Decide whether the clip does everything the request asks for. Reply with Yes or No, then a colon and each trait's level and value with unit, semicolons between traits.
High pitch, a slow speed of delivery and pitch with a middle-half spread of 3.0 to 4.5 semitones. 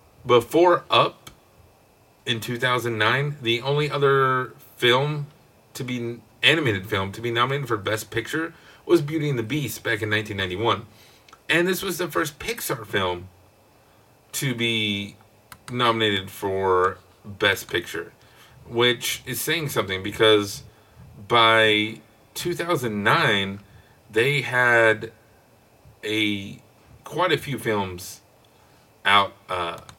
No: low, 115 Hz; slow, 120 wpm; average, 4.0 semitones